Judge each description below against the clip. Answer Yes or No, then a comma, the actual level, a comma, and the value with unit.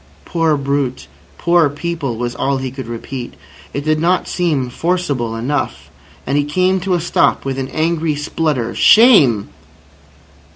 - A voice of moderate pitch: Yes, medium, 145 Hz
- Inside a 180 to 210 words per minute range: No, average, 150 wpm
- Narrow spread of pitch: No, average, 4.5 semitones